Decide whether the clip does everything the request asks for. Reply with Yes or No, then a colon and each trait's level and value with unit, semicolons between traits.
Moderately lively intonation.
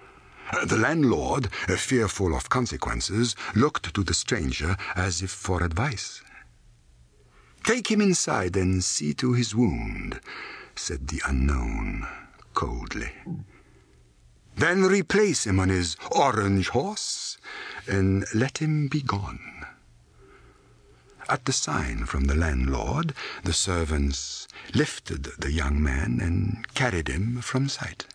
No: wide, 8.9 semitones